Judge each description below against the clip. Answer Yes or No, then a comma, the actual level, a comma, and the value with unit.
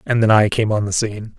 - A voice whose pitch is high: No, low, 110 Hz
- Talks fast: Yes, fast, 300 wpm